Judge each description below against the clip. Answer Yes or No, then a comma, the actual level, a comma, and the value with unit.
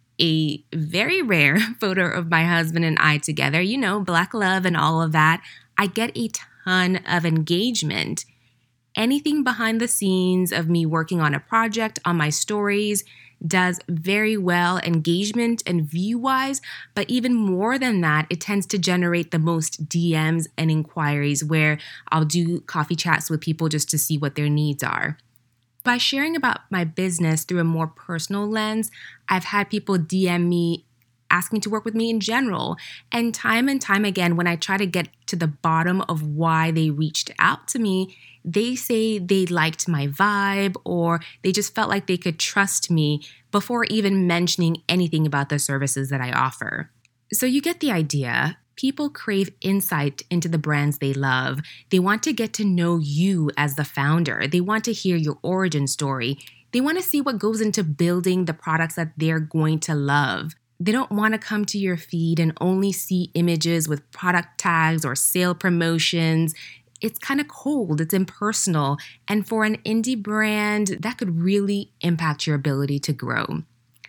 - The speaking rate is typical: Yes, average, 180 wpm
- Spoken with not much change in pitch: No, average, 4.6 semitones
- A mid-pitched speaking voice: Yes, medium, 175 Hz